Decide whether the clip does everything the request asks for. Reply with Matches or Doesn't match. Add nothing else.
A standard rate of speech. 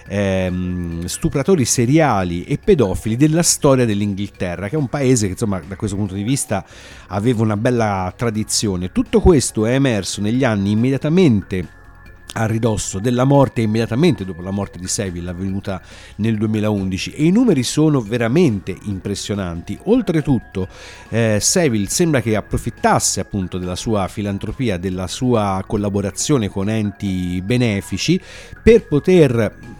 Matches